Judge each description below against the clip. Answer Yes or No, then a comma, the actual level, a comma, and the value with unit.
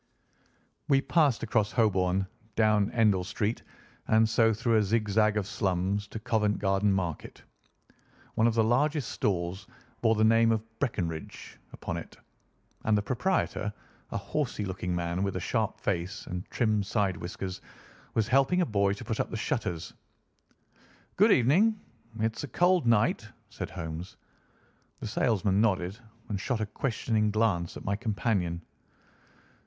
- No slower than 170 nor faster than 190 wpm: No, average, 150 wpm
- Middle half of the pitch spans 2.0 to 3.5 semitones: Yes, average, 2.9 semitones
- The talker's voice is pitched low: Yes, low, 105 Hz